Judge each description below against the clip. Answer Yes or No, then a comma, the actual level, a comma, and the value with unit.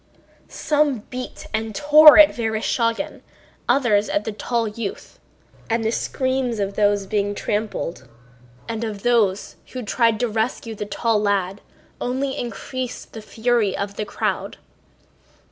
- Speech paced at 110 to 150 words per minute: Yes, average, 145 wpm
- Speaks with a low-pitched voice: No, high, 225 Hz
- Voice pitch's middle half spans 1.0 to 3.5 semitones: Yes, average, 3.1 semitones